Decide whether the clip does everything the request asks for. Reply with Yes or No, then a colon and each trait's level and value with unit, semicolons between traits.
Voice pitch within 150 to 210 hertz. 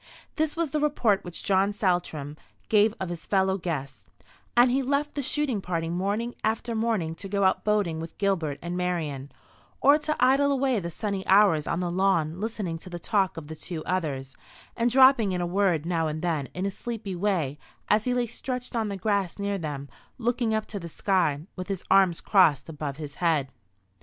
Yes: high, 190 Hz